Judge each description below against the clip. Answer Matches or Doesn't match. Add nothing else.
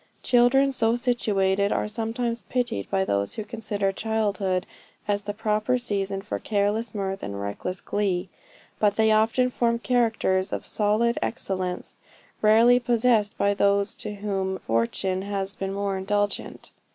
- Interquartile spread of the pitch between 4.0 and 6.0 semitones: Doesn't match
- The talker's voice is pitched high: Matches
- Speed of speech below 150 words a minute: Matches